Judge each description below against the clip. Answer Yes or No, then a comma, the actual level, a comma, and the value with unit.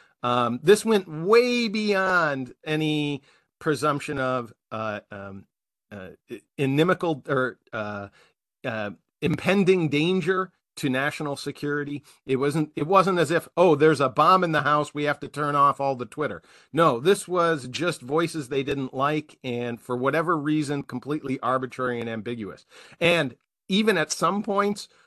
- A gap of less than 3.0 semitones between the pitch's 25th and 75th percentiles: No, average, 4.3 semitones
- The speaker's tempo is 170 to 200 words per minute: No, average, 150 wpm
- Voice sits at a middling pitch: Yes, medium, 150 Hz